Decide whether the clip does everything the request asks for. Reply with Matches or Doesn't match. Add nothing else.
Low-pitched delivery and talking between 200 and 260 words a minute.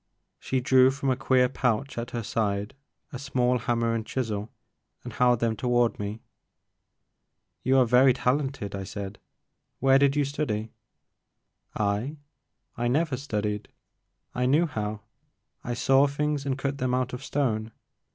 Doesn't match